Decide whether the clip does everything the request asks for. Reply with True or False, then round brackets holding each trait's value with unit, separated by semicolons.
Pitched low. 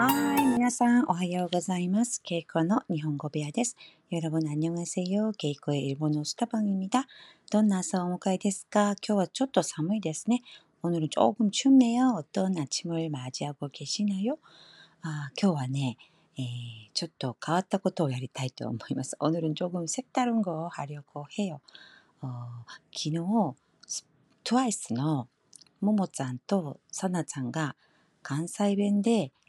False (175 Hz)